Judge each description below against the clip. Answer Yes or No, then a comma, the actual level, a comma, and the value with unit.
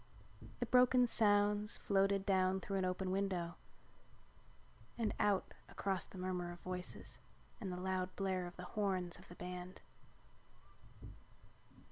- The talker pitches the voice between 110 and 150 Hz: No, high, 190 Hz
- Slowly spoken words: Yes, slow, 130 wpm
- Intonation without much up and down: Yes, narrow, 1.7 semitones